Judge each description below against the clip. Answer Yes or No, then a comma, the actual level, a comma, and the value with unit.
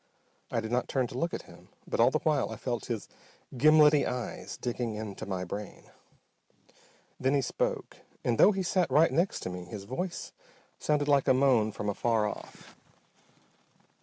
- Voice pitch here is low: Yes, low, 125 Hz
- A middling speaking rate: Yes, average, 175 wpm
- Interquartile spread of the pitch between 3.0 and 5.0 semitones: No, wide, 5.4 semitones